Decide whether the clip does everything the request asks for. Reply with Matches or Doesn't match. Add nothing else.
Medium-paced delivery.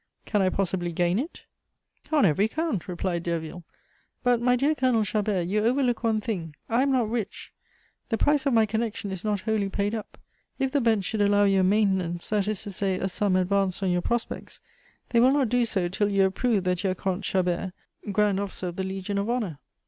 Doesn't match